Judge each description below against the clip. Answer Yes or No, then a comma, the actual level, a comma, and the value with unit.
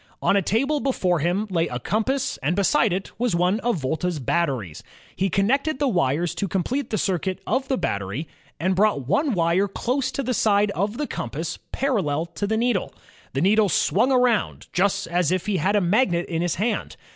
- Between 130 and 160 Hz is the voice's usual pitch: No, high, 195 Hz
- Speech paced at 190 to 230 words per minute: Yes, average, 195 wpm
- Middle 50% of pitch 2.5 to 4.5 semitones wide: No, wide, 5.4 semitones